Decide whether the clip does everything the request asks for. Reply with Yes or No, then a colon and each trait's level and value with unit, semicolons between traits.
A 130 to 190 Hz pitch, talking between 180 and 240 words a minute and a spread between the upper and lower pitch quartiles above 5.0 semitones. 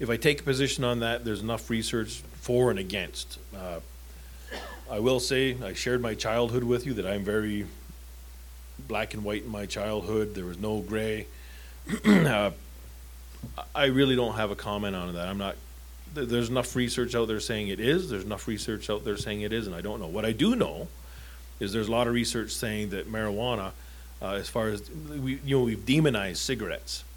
No: low, 105 Hz; average, 200 wpm; wide, 5.6 semitones